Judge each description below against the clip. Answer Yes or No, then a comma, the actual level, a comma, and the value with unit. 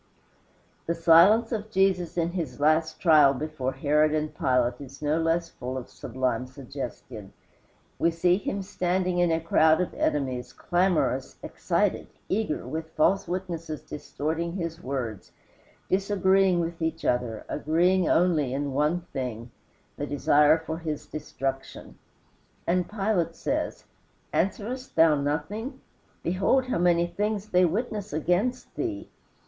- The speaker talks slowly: Yes, slow, 130 wpm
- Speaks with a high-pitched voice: No, medium, 165 Hz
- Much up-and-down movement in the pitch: No, average, 4.1 semitones